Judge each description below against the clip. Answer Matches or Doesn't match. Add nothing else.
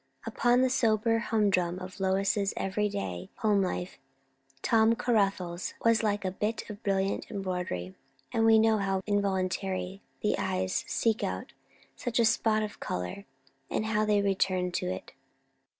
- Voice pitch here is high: Matches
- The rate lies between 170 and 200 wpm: Doesn't match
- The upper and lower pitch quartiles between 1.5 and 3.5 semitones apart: Matches